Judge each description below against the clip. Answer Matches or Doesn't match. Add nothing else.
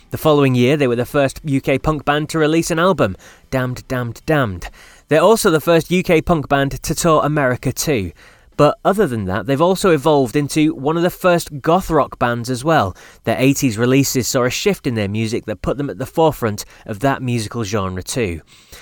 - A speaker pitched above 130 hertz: Matches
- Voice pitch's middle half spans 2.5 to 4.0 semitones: Doesn't match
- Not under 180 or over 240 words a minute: Matches